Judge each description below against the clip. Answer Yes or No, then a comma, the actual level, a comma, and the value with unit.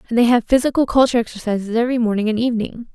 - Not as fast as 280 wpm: Yes, fast, 205 wpm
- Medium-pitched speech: No, high, 235 Hz